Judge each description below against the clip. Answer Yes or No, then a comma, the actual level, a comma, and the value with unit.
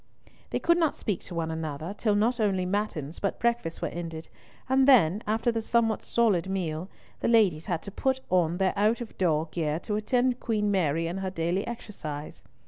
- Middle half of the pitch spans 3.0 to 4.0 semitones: No, wide, 5.4 semitones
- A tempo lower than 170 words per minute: No, average, 185 wpm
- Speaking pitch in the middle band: No, high, 195 Hz